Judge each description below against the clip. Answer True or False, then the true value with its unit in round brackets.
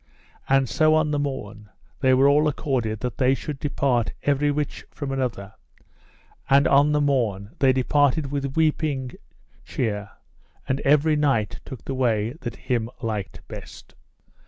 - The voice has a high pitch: False (135 Hz)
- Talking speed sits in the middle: True (145 wpm)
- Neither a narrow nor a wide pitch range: True (3.6 semitones)